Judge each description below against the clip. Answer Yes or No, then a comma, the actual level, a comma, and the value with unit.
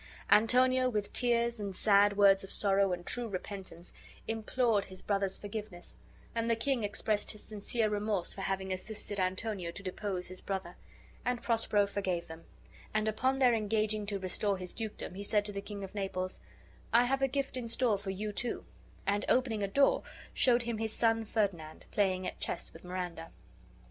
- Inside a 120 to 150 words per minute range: No, average, 180 wpm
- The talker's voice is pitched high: Yes, high, 205 Hz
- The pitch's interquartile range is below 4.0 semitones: Yes, average, 2.9 semitones